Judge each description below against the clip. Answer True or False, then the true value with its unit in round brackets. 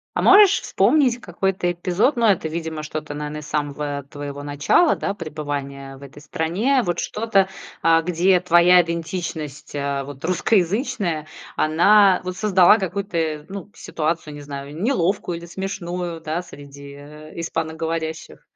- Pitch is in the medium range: True (165 Hz)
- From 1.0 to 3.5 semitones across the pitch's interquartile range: False (4.1 semitones)